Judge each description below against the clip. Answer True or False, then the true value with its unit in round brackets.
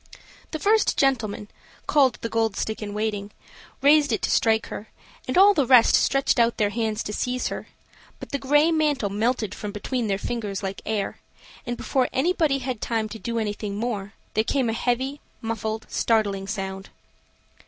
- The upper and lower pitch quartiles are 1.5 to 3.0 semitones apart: False (4.0 semitones)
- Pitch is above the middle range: True (225 Hz)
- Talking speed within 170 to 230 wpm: True (175 wpm)